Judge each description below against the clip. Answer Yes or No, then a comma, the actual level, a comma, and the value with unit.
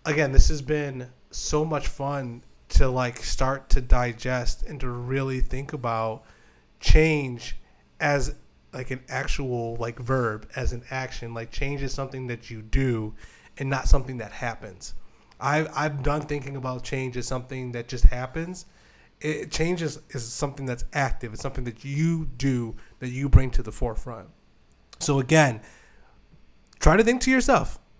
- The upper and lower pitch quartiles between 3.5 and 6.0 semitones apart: No, average, 2.9 semitones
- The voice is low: Yes, low, 130 Hz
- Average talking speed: Yes, average, 165 wpm